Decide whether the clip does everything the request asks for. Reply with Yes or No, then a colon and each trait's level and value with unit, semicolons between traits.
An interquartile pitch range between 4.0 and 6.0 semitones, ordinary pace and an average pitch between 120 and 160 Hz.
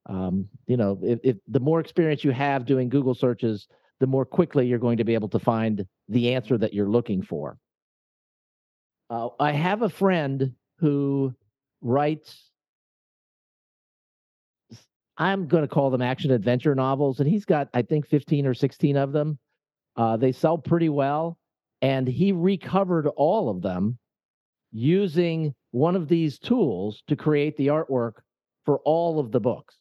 Yes: average, 4.3 semitones; average, 160 wpm; low, 135 Hz